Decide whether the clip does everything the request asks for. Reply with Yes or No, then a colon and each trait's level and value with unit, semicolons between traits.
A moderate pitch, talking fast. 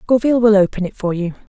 No: high, 205 Hz; fast, 230 wpm